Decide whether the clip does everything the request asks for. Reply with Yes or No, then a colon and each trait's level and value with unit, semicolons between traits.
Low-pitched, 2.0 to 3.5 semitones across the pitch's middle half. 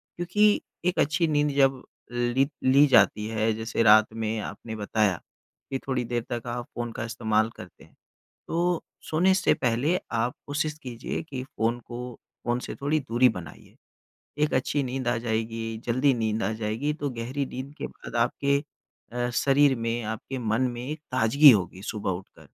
No: low, 120 Hz; average, 3.9 semitones